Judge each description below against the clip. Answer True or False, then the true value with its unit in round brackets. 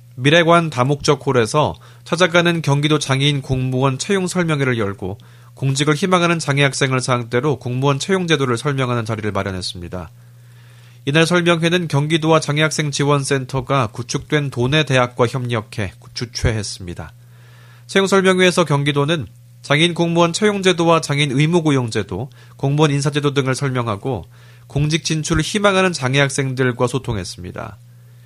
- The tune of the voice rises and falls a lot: False (4.4 semitones)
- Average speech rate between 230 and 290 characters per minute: False (355 characters per minute)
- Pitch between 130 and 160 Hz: True (140 Hz)